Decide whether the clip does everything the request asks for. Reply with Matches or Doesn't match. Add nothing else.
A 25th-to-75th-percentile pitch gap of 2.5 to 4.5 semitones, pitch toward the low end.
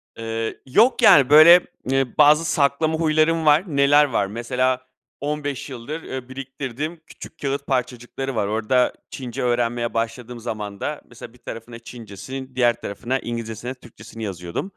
Matches